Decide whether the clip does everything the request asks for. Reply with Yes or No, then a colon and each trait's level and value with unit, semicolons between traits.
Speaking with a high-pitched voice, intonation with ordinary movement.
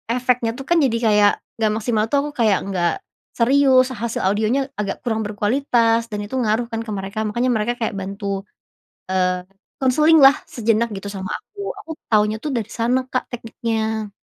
Yes: high, 225 Hz; average, 3.2 semitones